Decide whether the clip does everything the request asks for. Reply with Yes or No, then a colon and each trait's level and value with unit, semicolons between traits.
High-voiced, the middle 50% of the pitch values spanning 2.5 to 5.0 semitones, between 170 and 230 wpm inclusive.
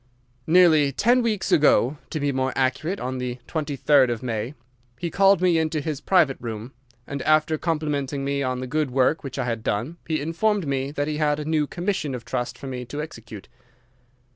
No: medium, 145 Hz; average, 3.7 semitones; average, 190 wpm